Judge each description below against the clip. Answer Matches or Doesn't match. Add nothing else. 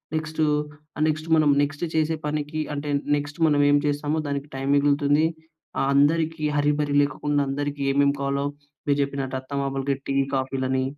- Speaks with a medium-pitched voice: Matches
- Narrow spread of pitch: Matches